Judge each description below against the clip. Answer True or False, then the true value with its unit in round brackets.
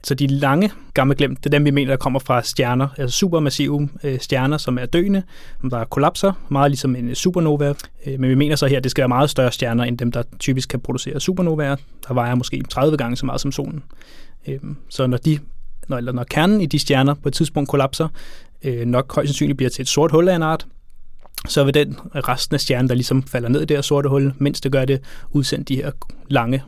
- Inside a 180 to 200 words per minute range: False (225 wpm)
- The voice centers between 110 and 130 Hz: False (140 Hz)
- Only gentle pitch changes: True (2.1 semitones)